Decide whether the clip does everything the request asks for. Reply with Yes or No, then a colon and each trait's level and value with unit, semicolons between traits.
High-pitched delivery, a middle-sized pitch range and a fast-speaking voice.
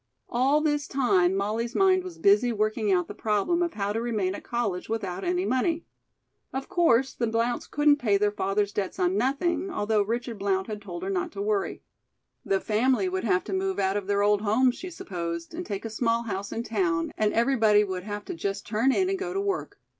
Yes: high, 215 Hz; average, 5.0 semitones; fast, 215 wpm